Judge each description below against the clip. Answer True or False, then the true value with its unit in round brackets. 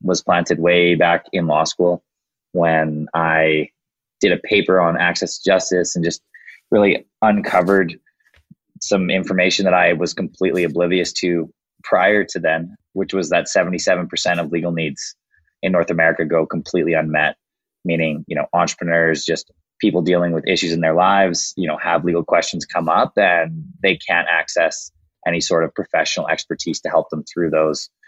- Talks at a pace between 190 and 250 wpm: False (165 wpm)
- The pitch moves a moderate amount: False (1.6 semitones)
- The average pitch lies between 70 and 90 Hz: True (85 Hz)